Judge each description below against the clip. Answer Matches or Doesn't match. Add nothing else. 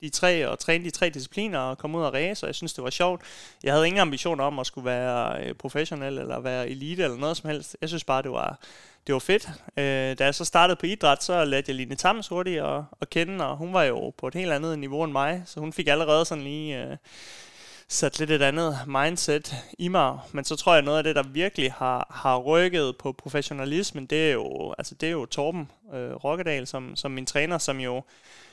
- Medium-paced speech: Doesn't match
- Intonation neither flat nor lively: Matches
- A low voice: Doesn't match